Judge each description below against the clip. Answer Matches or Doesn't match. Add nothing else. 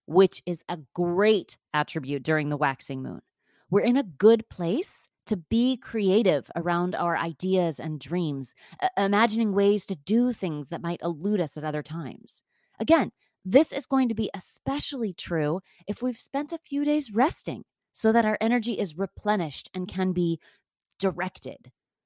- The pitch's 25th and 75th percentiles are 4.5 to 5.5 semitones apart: Matches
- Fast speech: Doesn't match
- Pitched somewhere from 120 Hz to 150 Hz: Doesn't match